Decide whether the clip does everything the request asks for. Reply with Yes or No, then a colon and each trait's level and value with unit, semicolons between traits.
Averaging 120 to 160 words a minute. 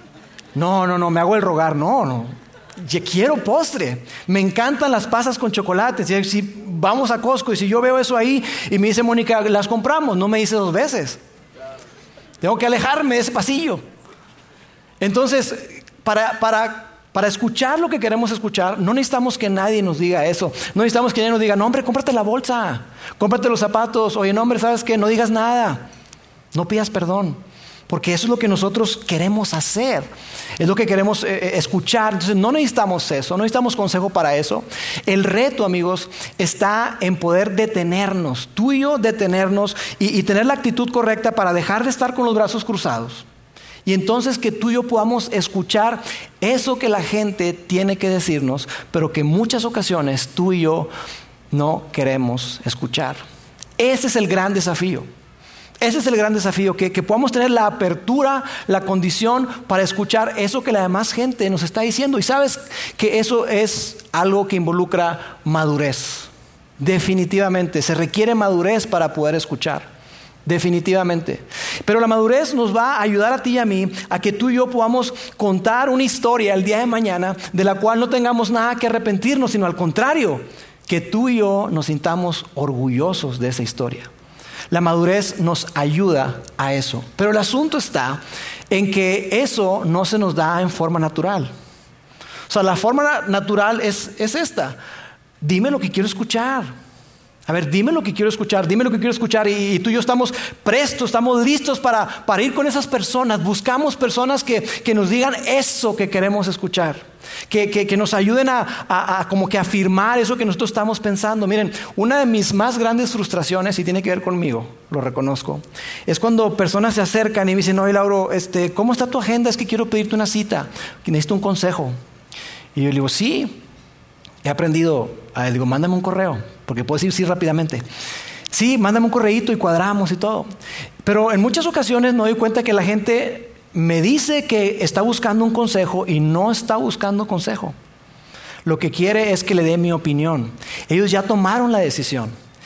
No: average, 185 wpm